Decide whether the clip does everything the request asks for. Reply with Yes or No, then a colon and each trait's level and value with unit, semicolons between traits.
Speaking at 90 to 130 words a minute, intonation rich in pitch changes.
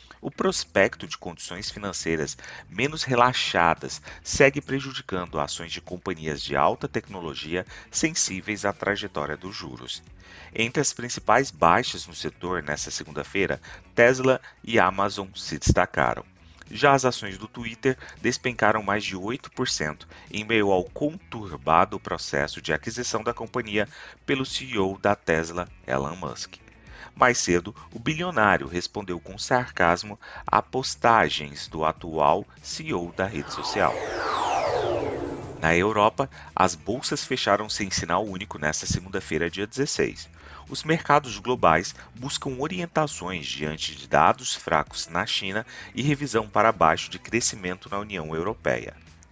Yes: average, 125 wpm; wide, 5.8 semitones